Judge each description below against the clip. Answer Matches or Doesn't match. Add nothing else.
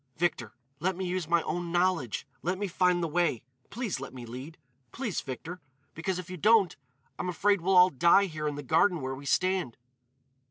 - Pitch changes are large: Doesn't match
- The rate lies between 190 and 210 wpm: Matches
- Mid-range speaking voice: Matches